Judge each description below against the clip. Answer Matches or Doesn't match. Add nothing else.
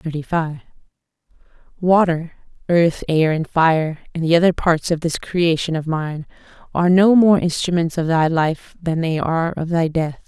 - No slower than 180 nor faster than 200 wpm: Doesn't match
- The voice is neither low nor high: Matches